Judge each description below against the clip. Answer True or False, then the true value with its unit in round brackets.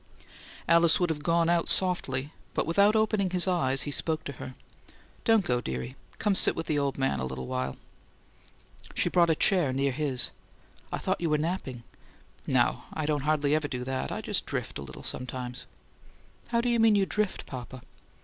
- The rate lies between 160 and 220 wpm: True (190 wpm)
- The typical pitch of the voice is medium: True (150 Hz)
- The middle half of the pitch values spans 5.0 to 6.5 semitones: True (5.5 semitones)